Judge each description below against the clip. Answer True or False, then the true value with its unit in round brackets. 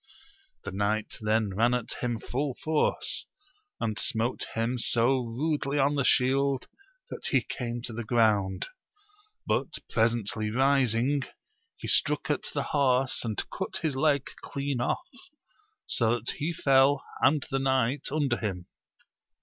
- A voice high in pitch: False (125 Hz)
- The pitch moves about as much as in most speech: True (3.5 semitones)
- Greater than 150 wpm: False (140 wpm)